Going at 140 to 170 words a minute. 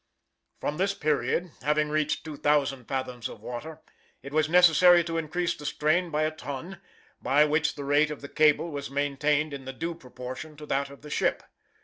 No: average, 180 wpm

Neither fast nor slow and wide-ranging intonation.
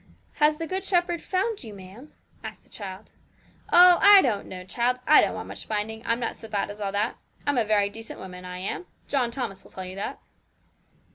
No: fast, 215 wpm; wide, 7.2 semitones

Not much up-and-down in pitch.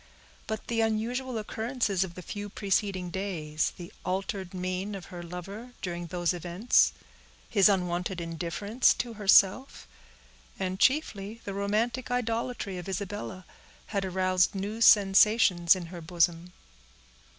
No: average, 3.4 semitones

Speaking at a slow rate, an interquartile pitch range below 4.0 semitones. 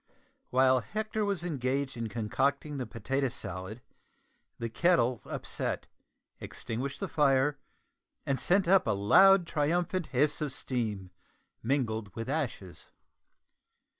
No: slow, 115 wpm; average, 5.0 semitones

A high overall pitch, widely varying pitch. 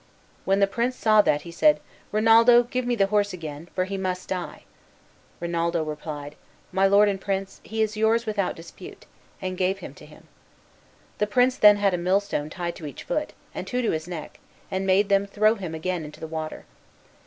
No: high, 195 Hz; average, 3.9 semitones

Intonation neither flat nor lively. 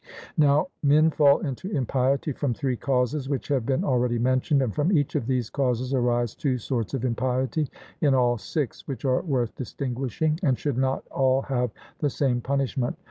No: narrow, 2.3 semitones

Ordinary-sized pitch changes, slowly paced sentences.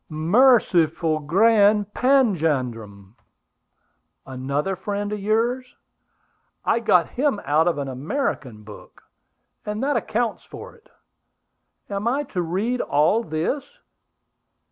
No: wide, 7.5 semitones; slow, 105 wpm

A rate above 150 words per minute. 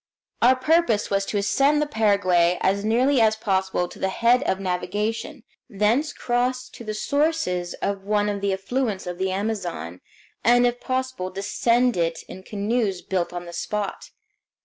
Yes: average, 165 wpm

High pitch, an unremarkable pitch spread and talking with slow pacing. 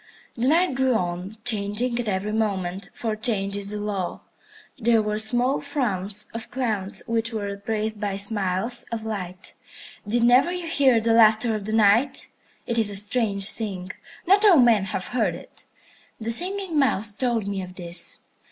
No: high, 220 Hz; average, 3.3 semitones; average, 170 wpm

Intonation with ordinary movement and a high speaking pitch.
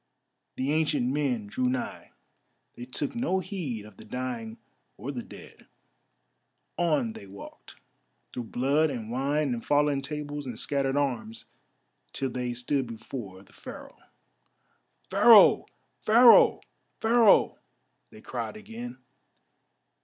No: average, 3.8 semitones; low, 135 Hz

